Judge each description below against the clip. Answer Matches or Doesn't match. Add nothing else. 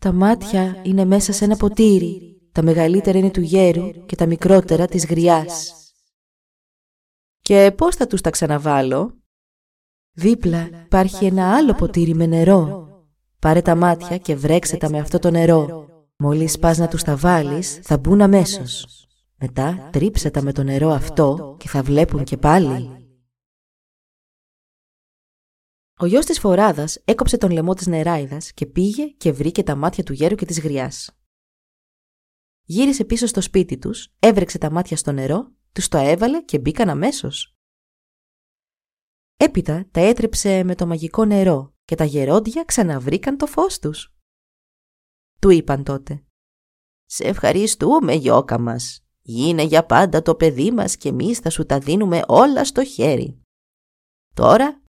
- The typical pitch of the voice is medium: Matches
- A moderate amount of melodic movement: Matches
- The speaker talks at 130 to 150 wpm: Matches